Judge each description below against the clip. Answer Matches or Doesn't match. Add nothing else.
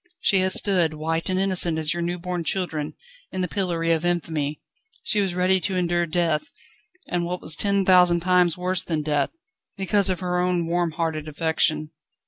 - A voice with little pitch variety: Matches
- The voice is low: Doesn't match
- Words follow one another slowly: Doesn't match